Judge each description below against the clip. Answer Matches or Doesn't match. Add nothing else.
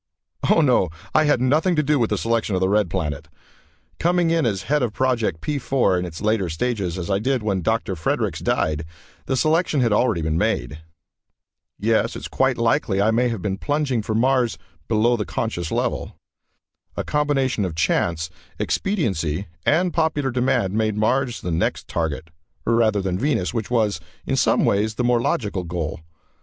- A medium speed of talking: Matches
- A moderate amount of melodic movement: Doesn't match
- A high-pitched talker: Doesn't match